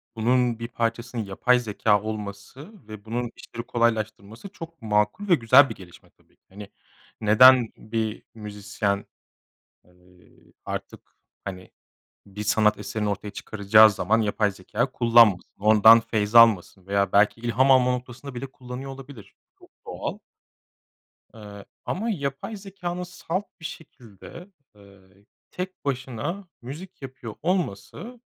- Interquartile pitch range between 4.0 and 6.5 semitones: Yes, average, 4.3 semitones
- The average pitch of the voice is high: No, low, 115 Hz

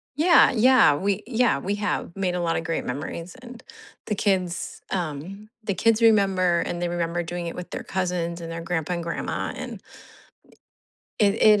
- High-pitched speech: No, medium, 180 Hz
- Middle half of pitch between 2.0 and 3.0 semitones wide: No, average, 3.7 semitones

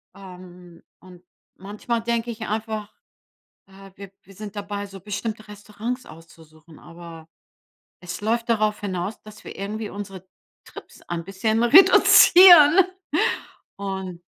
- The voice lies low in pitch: No, high, 200 Hz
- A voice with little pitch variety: No, average, 3.2 semitones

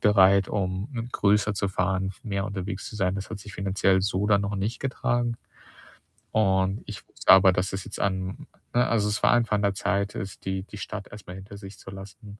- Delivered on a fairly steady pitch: Yes, narrow, 1.6 semitones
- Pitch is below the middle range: Yes, low, 100 Hz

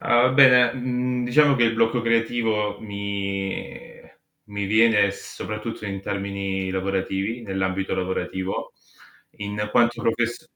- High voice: No, low, 105 Hz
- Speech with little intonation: No, average, 3.4 semitones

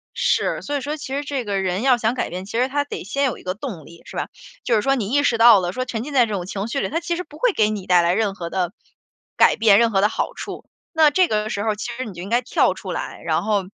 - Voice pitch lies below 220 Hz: No, high, 225 Hz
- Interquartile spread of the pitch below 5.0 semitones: No, wide, 5.6 semitones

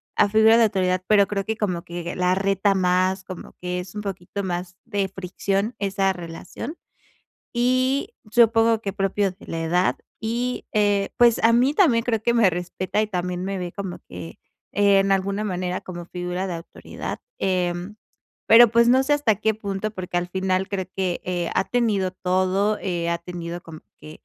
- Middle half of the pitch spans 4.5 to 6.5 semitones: No, average, 3.2 semitones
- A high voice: Yes, high, 195 Hz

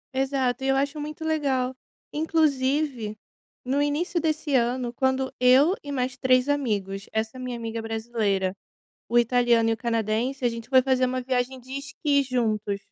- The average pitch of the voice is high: Yes, very high, 255 Hz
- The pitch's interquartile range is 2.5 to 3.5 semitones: Yes, average, 3.2 semitones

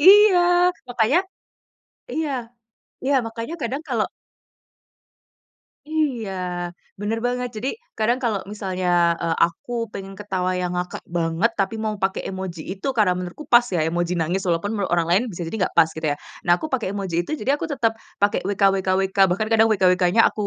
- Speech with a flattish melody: No, average, 4.5 semitones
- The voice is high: Yes, high, 200 Hz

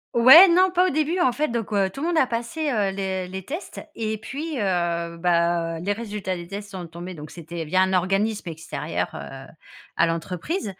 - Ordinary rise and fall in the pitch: No, wide, 6.7 semitones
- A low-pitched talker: No, high, 195 Hz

